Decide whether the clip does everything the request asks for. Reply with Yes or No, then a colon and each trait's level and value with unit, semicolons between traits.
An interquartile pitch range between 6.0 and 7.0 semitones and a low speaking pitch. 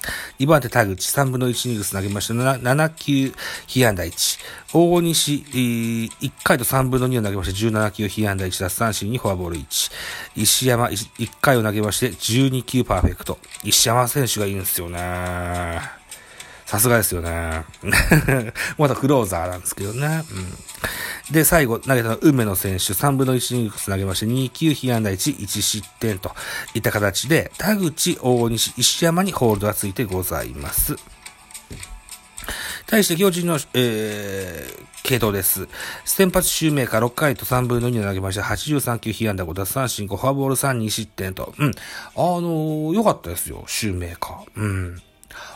No: wide, 5.4 semitones; low, 115 Hz